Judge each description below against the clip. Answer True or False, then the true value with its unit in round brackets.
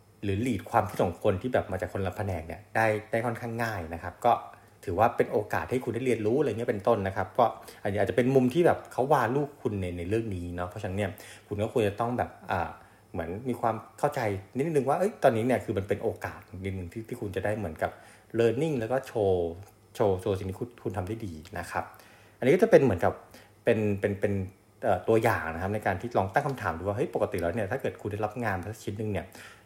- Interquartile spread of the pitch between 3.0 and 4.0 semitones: True (3.6 semitones)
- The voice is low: True (105 Hz)